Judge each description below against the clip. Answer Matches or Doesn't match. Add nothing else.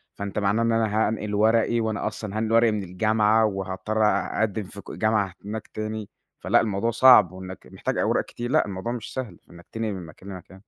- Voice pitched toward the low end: Matches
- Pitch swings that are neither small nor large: Doesn't match